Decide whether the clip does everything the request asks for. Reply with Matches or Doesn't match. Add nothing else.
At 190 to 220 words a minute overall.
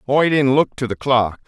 Doesn't match